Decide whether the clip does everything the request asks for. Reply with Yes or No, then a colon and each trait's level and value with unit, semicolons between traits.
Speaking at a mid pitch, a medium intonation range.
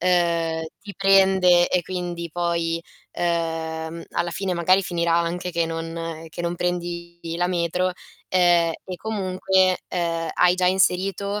No: medium, 175 Hz; narrow, 1.6 semitones